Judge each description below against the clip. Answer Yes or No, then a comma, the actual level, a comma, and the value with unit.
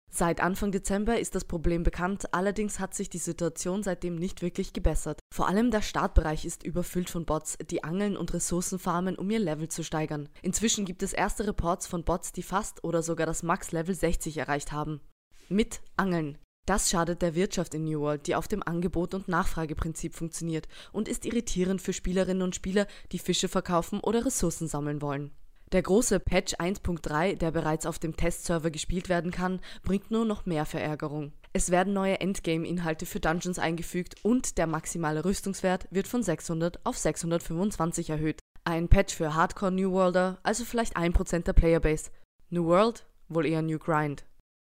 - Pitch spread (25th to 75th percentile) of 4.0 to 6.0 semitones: No, average, 2.7 semitones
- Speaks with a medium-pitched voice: Yes, medium, 175 Hz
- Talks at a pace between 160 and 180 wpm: Yes, average, 175 wpm